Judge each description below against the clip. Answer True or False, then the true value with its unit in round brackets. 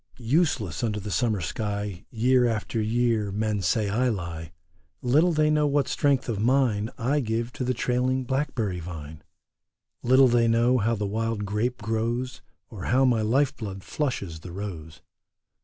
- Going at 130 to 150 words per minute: False (160 wpm)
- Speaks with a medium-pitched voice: False (115 Hz)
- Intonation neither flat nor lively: True (3.7 semitones)